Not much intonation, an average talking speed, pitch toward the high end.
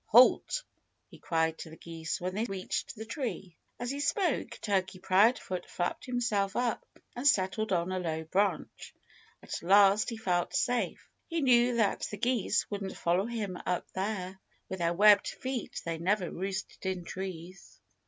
No: average, 4.4 semitones; average, 165 wpm; high, 195 Hz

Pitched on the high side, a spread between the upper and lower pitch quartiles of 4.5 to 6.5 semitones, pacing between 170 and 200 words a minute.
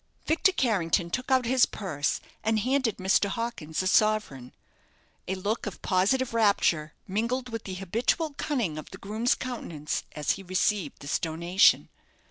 No: high, 205 Hz; wide, 5.4 semitones; average, 150 wpm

